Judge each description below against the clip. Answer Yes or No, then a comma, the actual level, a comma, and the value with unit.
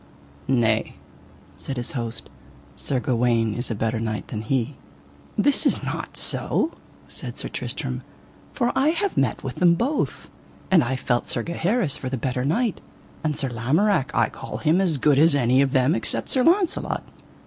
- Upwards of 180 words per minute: No, average, 170 wpm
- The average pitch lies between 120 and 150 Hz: Yes, low, 135 Hz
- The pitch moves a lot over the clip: Yes, wide, 7.0 semitones